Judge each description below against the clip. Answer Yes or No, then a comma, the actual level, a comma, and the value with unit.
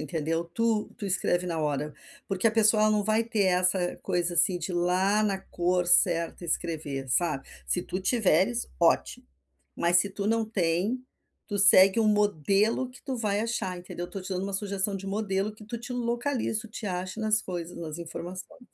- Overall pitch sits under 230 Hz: Yes, high, 190 Hz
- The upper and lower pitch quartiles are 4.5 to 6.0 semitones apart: No, average, 3.5 semitones